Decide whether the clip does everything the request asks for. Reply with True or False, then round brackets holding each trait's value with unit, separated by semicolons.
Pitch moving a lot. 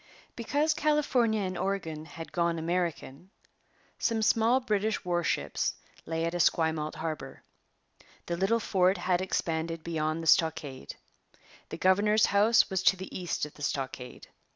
False (4.6 semitones)